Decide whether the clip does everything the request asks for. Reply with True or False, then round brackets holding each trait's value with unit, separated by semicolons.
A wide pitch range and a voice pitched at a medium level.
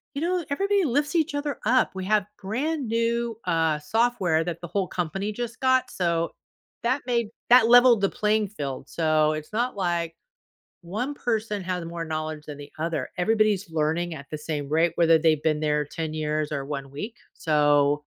True (7.0 semitones; 180 Hz)